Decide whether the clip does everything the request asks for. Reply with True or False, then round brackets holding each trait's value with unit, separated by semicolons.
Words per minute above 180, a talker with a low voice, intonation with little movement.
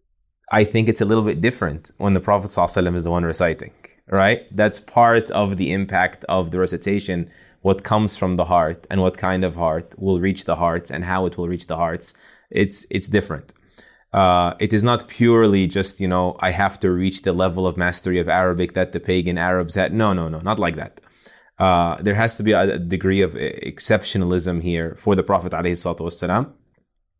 True (200 wpm; 95 Hz; 2.3 semitones)